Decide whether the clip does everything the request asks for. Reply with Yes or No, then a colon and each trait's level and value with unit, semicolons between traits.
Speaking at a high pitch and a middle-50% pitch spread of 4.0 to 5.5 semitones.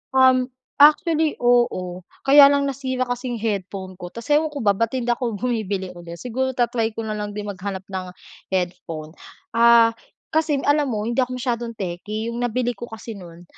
Yes: high, 235 Hz; average, 4.3 semitones